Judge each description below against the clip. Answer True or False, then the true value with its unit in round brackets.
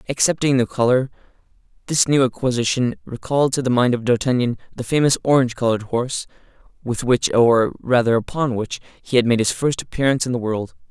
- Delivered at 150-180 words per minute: True (175 wpm)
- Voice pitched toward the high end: False (125 Hz)